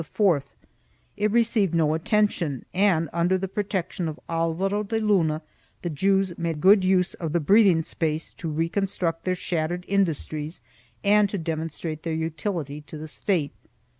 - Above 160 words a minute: No, average, 150 wpm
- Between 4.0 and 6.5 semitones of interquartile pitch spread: No, average, 3.6 semitones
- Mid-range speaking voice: Yes, medium, 170 Hz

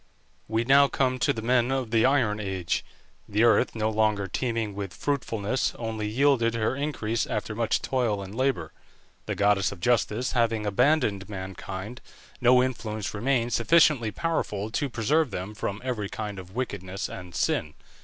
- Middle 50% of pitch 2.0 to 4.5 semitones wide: Yes, average, 3.8 semitones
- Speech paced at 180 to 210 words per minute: No, average, 160 wpm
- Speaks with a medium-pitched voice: No, low, 110 Hz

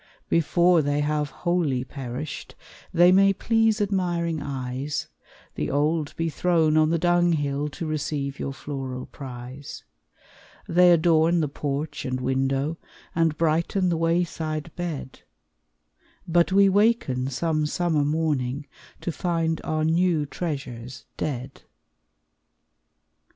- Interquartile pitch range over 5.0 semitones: No, average, 3.7 semitones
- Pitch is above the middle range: No, medium, 155 Hz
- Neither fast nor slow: No, slow, 115 wpm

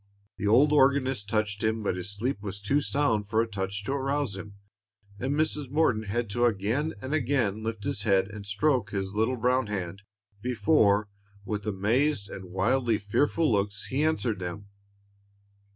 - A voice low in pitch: Yes, low, 110 Hz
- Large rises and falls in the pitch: No, average, 4.7 semitones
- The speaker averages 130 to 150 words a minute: No, average, 170 wpm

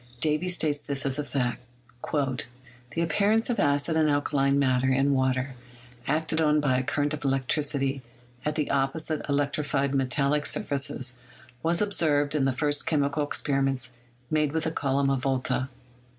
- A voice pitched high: No, medium, 140 Hz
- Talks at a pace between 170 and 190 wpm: No, average, 155 wpm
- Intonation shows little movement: Yes, narrow, 2.1 semitones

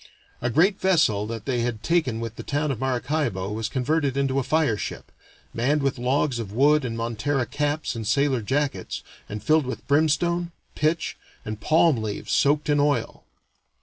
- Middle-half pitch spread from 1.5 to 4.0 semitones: No, average, 4.7 semitones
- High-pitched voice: No, low, 135 Hz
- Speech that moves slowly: No, average, 175 wpm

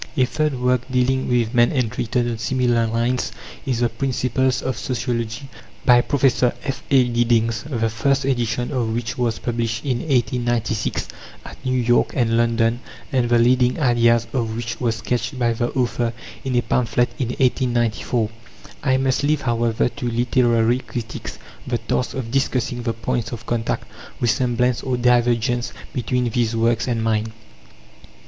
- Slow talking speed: No, average, 155 wpm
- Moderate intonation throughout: No, narrow, 1.6 semitones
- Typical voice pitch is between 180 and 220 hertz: No, low, 120 Hz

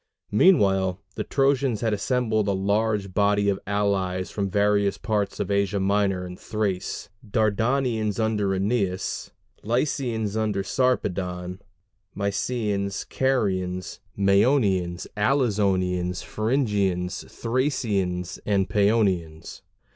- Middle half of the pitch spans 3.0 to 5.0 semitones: No, narrow, 2.6 semitones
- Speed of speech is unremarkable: No, slow, 95 wpm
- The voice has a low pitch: Yes, low, 100 Hz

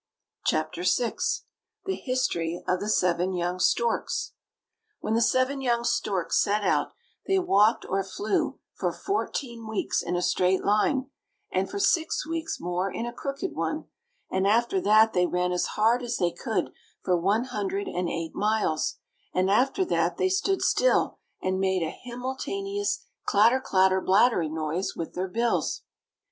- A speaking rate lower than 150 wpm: No, average, 155 wpm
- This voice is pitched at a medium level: No, high, 210 Hz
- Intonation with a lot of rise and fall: Yes, wide, 5.8 semitones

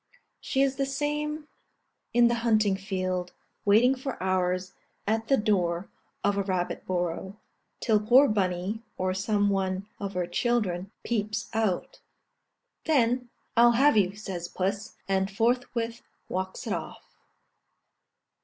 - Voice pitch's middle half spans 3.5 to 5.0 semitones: Yes, average, 4.1 semitones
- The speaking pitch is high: Yes, high, 205 Hz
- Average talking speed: No, slow, 130 wpm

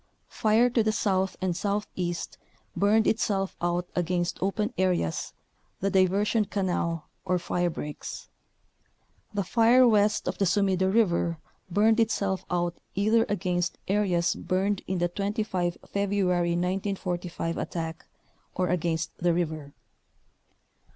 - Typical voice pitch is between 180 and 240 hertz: Yes, high, 190 Hz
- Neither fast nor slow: No, slow, 120 wpm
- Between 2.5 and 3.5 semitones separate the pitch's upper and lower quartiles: Yes, average, 2.8 semitones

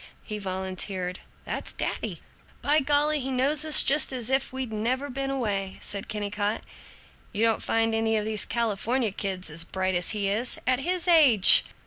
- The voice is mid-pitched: No, high, 225 Hz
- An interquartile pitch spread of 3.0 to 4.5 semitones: No, average, 5.0 semitones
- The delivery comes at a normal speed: Yes, average, 170 wpm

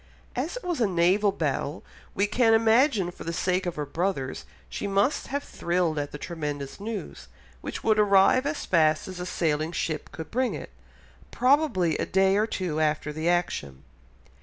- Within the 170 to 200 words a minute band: Yes, average, 175 wpm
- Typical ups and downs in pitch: No, wide, 5.7 semitones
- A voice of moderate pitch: Yes, medium, 180 Hz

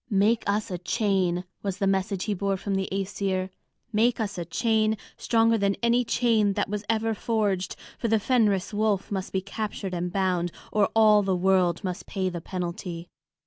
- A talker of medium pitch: No, high, 200 Hz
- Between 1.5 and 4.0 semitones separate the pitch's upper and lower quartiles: Yes, narrow, 2.6 semitones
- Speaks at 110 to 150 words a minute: No, average, 185 wpm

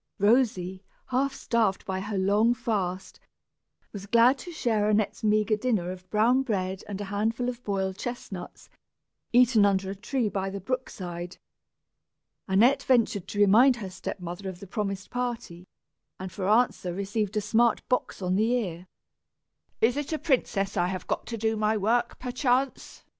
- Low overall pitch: No, high, 210 Hz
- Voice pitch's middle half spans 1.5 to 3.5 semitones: No, average, 4.0 semitones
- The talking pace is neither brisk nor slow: Yes, average, 165 wpm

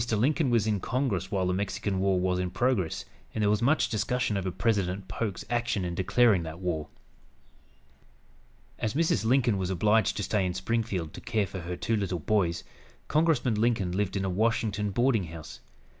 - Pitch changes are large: No, average, 3.8 semitones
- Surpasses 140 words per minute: Yes, average, 180 wpm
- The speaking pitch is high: No, low, 105 Hz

